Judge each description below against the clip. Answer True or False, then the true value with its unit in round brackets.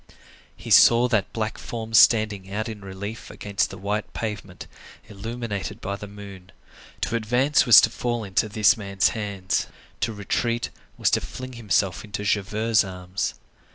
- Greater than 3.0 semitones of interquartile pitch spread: False (2.5 semitones)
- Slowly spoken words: False (155 wpm)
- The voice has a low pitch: True (105 Hz)